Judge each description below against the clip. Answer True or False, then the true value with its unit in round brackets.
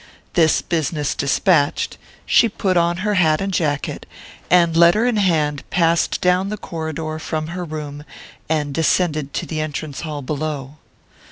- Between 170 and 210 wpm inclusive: False (150 wpm)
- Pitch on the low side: False (160 Hz)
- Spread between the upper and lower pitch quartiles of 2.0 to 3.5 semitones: True (3.0 semitones)